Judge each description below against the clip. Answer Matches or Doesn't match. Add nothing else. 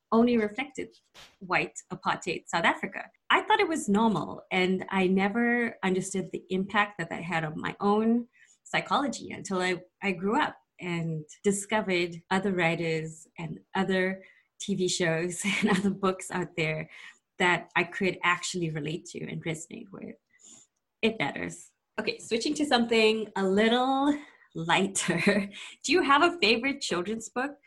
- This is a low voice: Doesn't match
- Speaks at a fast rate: Doesn't match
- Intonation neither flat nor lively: Matches